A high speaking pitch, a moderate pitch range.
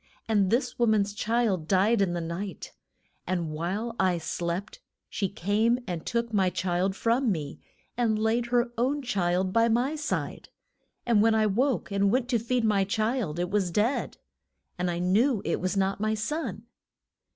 Yes: high, 210 Hz; average, 4.1 semitones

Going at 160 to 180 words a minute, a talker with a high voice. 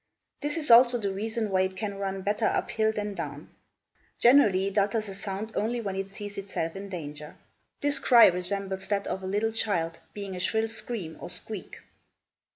No: average, 190 wpm; high, 200 Hz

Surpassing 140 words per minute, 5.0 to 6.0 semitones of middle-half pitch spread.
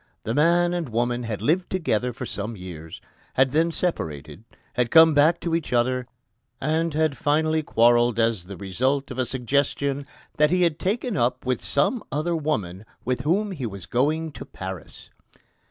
Yes: average, 170 wpm; wide, 5.5 semitones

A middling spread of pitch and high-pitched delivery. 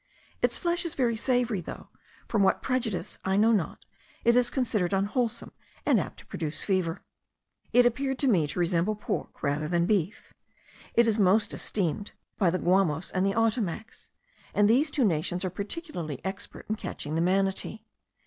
Yes: average, 4.8 semitones; high, 205 Hz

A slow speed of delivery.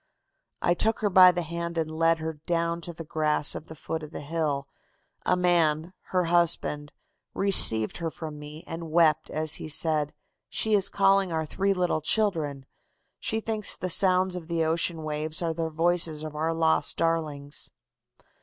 No: average, 175 wpm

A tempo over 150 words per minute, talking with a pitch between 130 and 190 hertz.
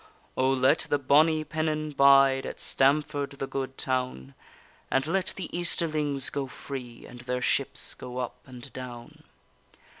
No: average, 145 wpm; low, 135 Hz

